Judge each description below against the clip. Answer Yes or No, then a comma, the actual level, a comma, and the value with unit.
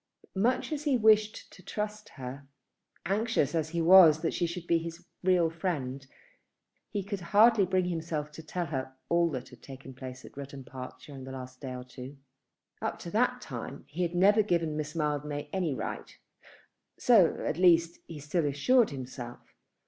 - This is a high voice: No, medium, 165 Hz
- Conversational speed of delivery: Yes, average, 180 wpm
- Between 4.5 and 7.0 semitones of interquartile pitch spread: Yes, average, 5.0 semitones